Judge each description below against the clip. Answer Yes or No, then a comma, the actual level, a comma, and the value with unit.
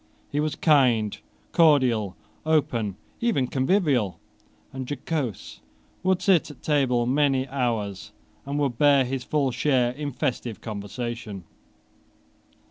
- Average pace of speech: No, slow, 115 wpm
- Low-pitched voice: Yes, low, 130 Hz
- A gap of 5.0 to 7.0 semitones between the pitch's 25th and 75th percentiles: No, average, 3.8 semitones